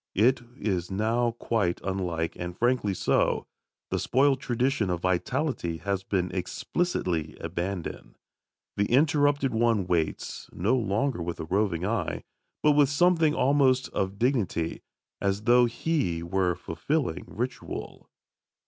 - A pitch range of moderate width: No, wide, 6.5 semitones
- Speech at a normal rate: No, slow, 125 wpm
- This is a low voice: Yes, low, 105 Hz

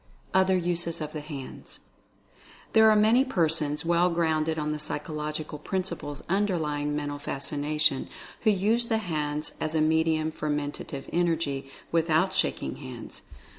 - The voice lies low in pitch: No, medium, 155 Hz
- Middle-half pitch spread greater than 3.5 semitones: No, average, 3.0 semitones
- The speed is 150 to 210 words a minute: No, average, 140 wpm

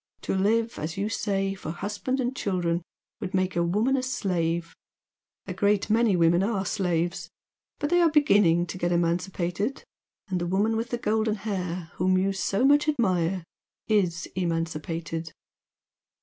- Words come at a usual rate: Yes, average, 150 wpm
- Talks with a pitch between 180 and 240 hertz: Yes, high, 190 Hz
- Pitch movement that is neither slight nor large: Yes, average, 4.0 semitones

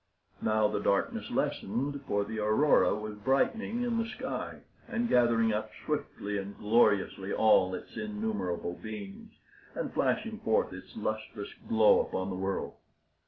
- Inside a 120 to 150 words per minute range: Yes, average, 140 wpm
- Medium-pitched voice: No, low, 110 Hz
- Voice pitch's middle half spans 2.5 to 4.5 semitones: No, average, 5.2 semitones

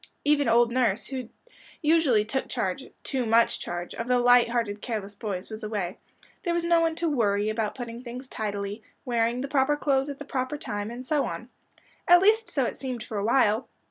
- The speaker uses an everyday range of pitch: Yes, average, 4.2 semitones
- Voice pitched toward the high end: Yes, high, 240 Hz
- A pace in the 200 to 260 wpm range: Yes, fast, 205 wpm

